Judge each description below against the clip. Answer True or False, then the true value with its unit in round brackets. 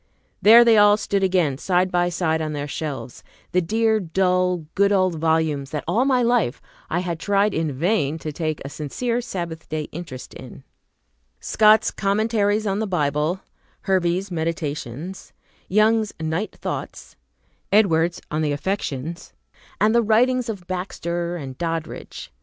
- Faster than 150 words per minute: False (145 wpm)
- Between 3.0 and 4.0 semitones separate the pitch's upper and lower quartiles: False (4.6 semitones)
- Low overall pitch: False (180 Hz)